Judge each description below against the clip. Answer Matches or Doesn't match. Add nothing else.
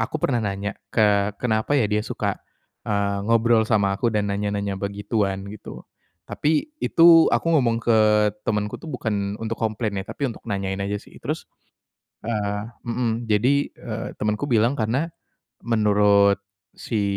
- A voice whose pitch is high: Doesn't match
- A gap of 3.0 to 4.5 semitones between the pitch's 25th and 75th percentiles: Doesn't match